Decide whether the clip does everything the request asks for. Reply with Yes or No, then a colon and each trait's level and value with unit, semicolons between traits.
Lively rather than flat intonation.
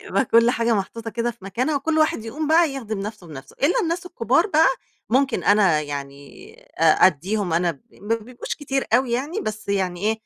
Yes: wide, 6.0 semitones